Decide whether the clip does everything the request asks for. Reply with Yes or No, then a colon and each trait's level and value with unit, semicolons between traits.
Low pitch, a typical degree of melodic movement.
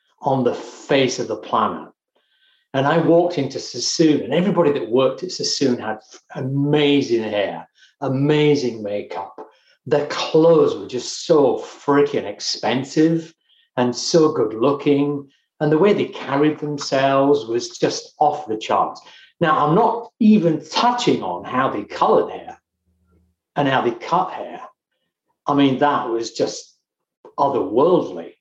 No: medium, 145 Hz; average, 4.7 semitones